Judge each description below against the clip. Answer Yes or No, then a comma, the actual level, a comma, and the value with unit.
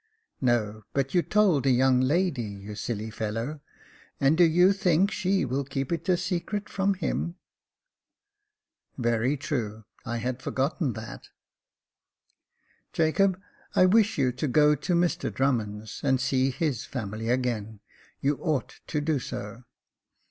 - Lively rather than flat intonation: Yes, wide, 6.3 semitones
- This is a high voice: No, low, 135 Hz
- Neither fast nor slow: Yes, average, 145 wpm